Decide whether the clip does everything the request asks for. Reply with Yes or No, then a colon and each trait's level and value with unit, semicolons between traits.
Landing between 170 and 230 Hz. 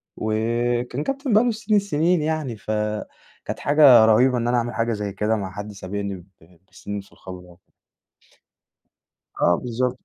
No: low, 115 Hz